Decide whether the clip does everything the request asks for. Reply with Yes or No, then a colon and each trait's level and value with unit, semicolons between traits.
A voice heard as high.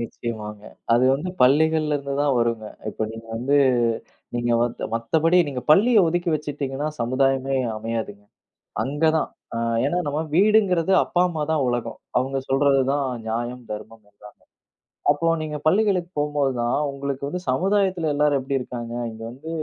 No: medium, 140 Hz